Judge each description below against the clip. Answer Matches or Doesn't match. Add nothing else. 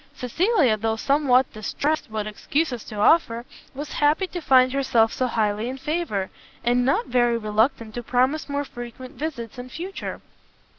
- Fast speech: Doesn't match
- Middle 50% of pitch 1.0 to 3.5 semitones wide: Doesn't match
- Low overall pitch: Doesn't match